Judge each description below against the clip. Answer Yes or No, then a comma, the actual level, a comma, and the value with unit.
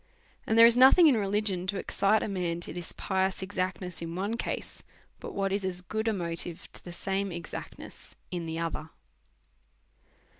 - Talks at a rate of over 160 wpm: Yes, average, 185 wpm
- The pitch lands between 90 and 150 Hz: No, high, 190 Hz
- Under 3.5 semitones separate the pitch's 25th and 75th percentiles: Yes, average, 2.9 semitones